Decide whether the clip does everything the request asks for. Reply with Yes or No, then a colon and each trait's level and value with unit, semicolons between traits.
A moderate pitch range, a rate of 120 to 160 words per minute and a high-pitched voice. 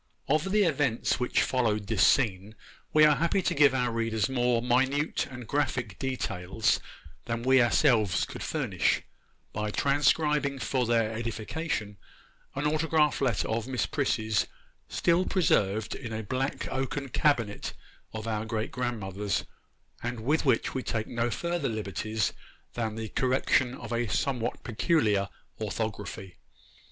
No: average, 4.0 semitones; average, 140 wpm; low, 120 Hz